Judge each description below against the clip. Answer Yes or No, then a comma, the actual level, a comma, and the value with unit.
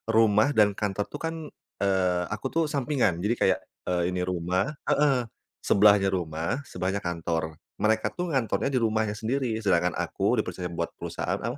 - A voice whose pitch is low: Yes, low, 100 Hz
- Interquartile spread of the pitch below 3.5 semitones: No, average, 3.9 semitones